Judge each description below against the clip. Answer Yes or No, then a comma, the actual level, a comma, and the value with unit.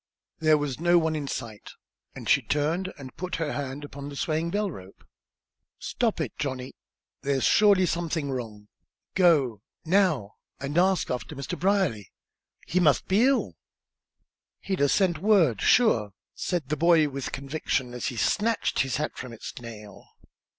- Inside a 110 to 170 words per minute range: Yes, average, 155 wpm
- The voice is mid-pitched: Yes, medium, 150 Hz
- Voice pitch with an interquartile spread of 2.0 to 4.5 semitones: No, average, 5.3 semitones